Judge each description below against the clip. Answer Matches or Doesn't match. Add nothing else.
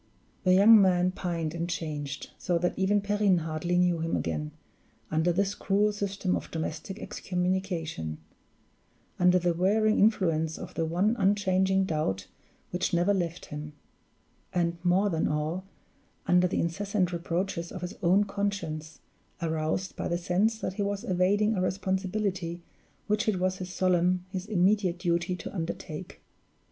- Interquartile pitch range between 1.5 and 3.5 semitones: Matches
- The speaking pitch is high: Doesn't match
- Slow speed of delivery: Doesn't match